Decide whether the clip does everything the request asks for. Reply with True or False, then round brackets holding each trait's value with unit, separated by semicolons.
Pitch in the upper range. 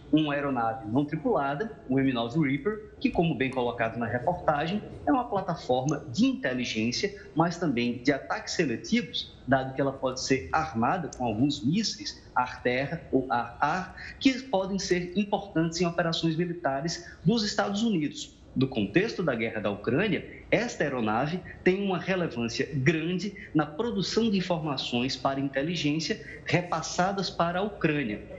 False (160 Hz)